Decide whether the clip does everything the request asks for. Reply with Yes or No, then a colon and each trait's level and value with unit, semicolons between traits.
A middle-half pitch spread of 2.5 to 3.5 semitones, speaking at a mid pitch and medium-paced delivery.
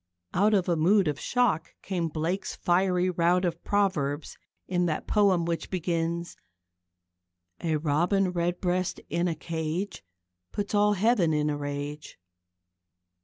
No: average, 3.0 semitones; medium, 175 Hz; slow, 130 wpm